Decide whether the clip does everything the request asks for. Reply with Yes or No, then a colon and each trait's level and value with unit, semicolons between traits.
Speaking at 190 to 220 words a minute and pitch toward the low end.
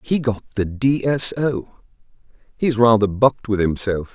No: average, 160 wpm; low, 115 Hz